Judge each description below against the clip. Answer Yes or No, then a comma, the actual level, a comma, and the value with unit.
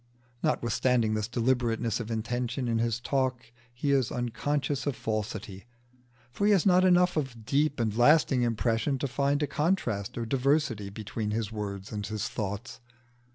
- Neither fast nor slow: Yes, average, 155 wpm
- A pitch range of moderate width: Yes, average, 4.1 semitones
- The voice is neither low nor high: No, low, 120 Hz